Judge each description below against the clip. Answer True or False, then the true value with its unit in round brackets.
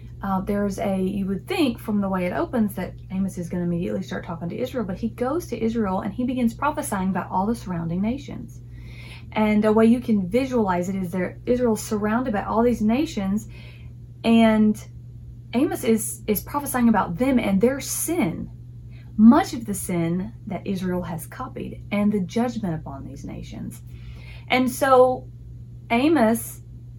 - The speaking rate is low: False (170 wpm)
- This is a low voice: False (195 Hz)